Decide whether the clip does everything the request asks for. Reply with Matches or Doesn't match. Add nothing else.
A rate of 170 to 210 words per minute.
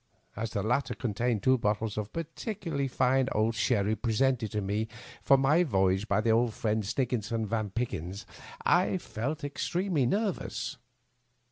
Doesn't match